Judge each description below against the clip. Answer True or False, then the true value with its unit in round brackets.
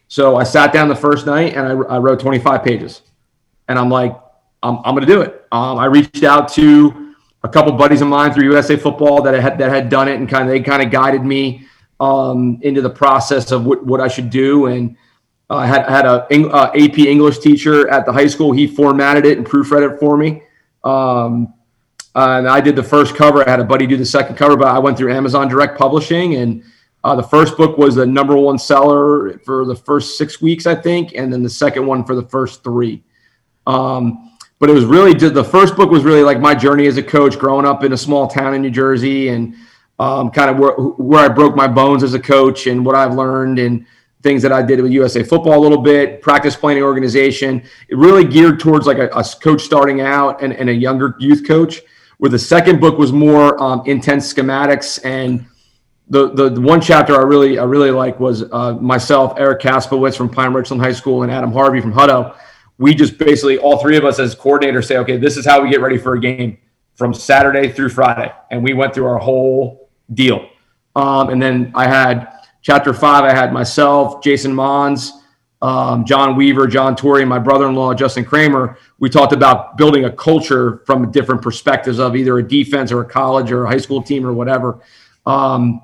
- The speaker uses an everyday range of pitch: False (1.9 semitones)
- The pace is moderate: False (220 wpm)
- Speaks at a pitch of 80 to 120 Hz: False (135 Hz)